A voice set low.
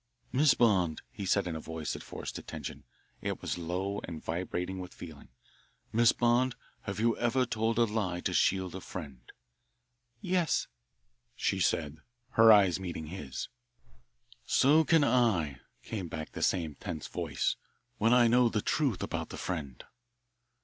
Yes: very low, 95 Hz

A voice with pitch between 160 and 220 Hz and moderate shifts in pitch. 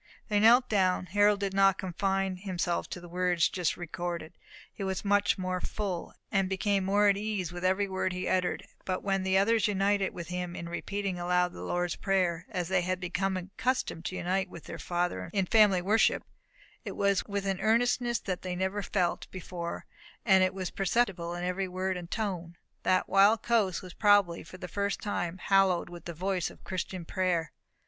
No: medium, 185 Hz; narrow, 2.0 semitones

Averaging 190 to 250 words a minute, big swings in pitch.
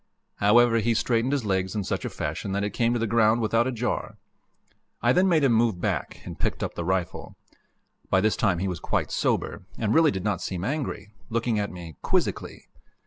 No: fast, 205 wpm; average, 3.6 semitones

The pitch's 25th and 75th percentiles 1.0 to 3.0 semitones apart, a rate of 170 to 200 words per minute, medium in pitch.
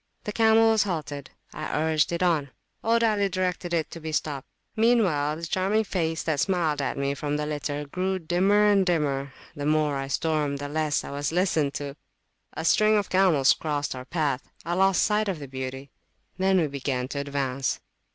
No: average, 4.8 semitones; average, 185 wpm; medium, 155 Hz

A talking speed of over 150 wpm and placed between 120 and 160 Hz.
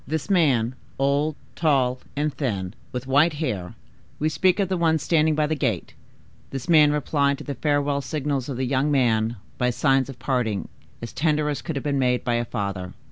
Yes: average, 190 wpm; medium, 140 Hz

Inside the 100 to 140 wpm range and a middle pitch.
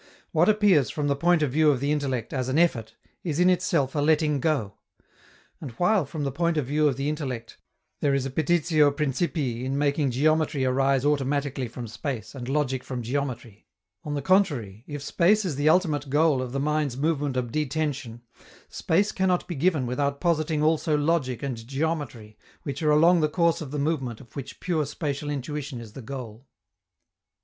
No: average, 190 wpm; medium, 145 Hz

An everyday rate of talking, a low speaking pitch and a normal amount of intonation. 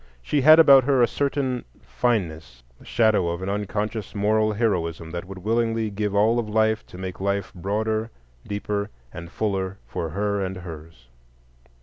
Yes: average, 160 wpm; low, 105 Hz; average, 3.3 semitones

